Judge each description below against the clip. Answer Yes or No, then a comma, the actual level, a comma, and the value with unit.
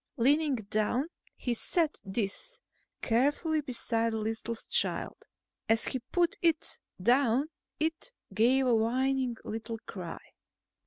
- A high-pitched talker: Yes, high, 245 Hz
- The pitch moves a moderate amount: Yes, average, 4.4 semitones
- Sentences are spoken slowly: Yes, slow, 115 wpm